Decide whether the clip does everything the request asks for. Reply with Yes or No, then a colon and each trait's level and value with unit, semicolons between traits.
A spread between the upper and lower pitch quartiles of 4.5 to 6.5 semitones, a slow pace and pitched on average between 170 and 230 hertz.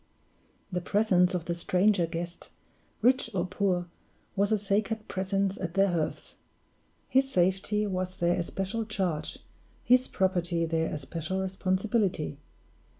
No: average, 2.7 semitones; slow, 125 wpm; medium, 185 Hz